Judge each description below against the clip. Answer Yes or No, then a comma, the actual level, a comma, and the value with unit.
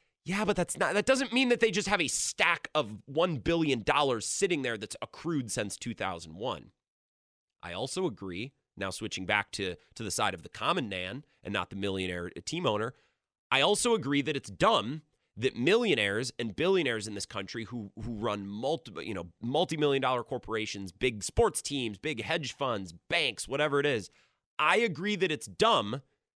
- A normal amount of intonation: No, wide, 7.8 semitones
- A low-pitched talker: Yes, low, 125 Hz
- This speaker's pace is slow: No, average, 190 wpm